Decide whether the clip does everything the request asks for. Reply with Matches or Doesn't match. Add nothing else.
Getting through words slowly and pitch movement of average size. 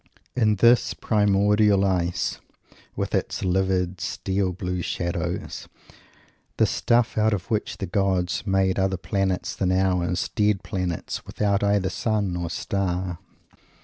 Doesn't match